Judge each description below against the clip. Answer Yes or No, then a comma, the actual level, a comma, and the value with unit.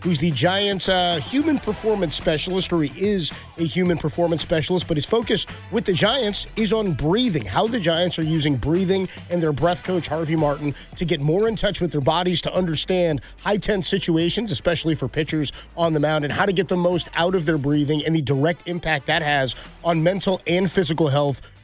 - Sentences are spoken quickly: Yes, fast, 210 wpm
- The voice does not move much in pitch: No, average, 3.4 semitones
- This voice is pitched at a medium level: Yes, medium, 170 Hz